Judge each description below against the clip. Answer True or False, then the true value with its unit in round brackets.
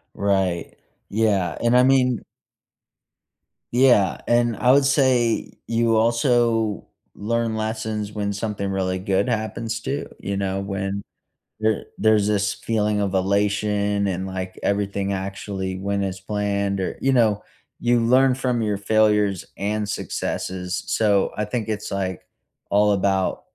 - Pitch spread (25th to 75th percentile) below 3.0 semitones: True (2.6 semitones)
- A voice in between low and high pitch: False (105 Hz)